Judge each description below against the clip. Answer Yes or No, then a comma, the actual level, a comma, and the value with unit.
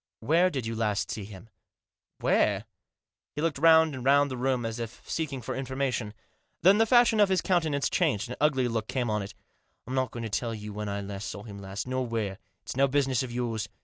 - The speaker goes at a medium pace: No, fast, 240 wpm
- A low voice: Yes, low, 125 Hz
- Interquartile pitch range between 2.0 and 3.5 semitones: No, average, 4.6 semitones